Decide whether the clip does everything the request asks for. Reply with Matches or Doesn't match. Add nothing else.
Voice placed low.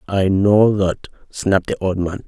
Matches